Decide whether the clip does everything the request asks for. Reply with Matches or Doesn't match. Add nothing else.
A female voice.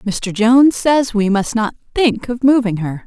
Matches